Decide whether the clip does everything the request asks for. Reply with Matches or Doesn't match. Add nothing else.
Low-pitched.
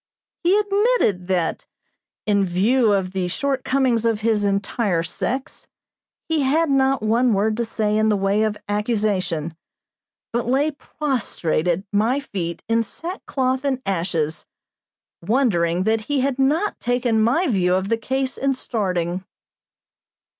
Doesn't match